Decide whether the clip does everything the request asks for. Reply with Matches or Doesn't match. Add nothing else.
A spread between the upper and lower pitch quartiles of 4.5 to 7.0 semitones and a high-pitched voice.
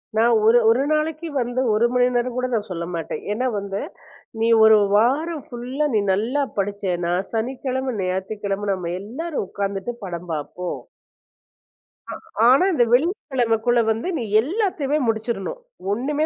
Matches